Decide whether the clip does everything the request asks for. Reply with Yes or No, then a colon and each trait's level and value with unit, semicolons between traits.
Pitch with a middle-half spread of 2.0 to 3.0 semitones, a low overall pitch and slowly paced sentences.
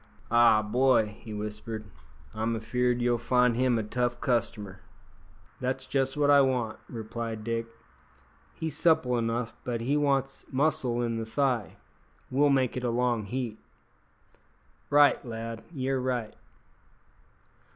Yes: narrow, 2.6 semitones; low, 120 Hz; slow, 130 wpm